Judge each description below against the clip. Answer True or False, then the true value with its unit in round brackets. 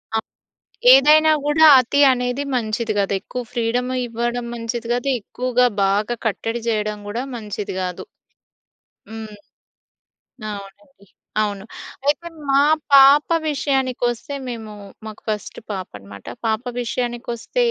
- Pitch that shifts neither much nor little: True (3.3 semitones)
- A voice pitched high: True (235 Hz)